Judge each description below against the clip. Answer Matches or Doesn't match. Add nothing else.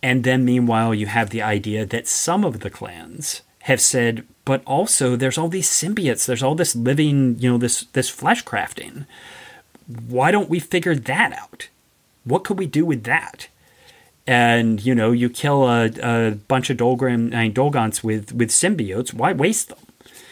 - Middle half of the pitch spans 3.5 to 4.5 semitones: Matches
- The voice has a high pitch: Doesn't match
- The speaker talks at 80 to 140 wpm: Doesn't match